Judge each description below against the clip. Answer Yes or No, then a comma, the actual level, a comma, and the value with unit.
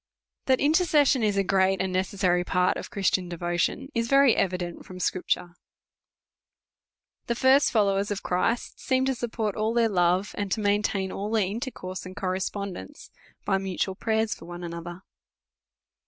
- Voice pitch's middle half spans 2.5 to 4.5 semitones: Yes, average, 3.7 semitones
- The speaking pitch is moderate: No, high, 195 Hz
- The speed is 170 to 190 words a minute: No, average, 155 wpm